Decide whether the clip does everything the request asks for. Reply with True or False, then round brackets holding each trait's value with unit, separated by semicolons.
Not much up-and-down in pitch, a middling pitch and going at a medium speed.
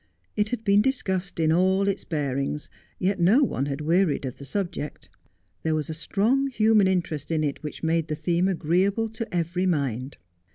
False (4.6 semitones; 175 Hz; 180 wpm)